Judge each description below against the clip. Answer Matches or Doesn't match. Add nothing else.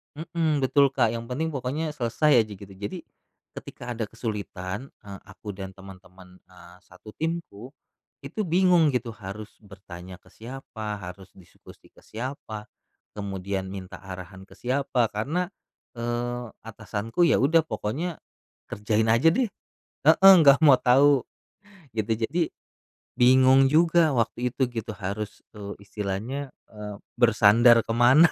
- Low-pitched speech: Matches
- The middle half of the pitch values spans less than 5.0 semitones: Doesn't match